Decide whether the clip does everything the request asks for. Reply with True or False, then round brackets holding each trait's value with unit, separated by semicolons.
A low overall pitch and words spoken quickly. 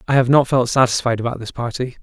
True (125 Hz; 235 wpm)